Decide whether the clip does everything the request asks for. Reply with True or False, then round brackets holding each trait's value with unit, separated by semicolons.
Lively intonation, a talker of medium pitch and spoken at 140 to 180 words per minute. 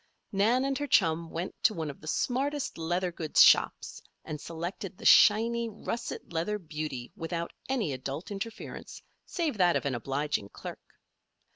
True (6.3 semitones; 175 Hz; 155 wpm)